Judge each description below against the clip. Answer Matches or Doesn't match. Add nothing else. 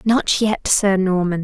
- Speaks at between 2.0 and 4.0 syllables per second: Matches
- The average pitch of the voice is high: Matches